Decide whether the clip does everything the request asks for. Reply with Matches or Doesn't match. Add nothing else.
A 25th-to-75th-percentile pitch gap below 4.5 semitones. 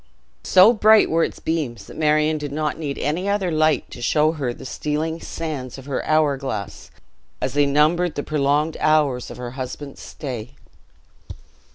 Matches